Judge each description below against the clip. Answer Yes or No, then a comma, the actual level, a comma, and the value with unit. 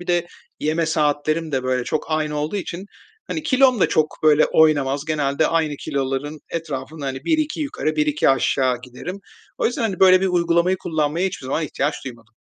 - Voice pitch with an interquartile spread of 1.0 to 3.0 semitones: No, average, 3.9 semitones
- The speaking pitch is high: No, medium, 155 Hz